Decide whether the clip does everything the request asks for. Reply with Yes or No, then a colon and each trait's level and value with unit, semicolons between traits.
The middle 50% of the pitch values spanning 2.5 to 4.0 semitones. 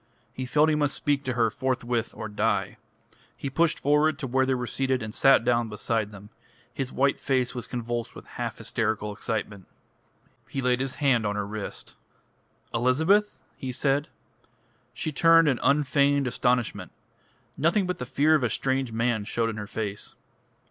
Yes: average, 3.6 semitones